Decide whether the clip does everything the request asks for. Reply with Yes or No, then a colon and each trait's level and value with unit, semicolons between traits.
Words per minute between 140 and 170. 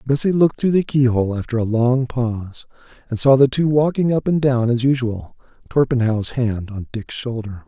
No: average, 190 wpm